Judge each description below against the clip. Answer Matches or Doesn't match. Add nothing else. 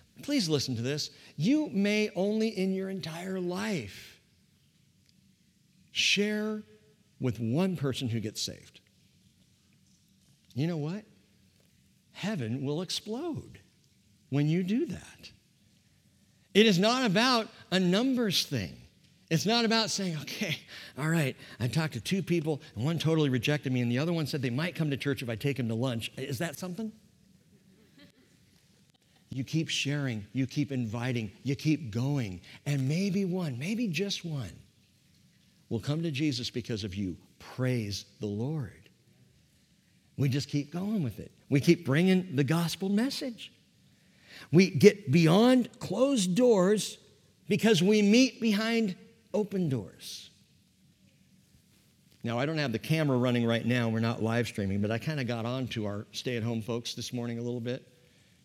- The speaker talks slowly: Doesn't match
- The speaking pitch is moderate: Matches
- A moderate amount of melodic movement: Doesn't match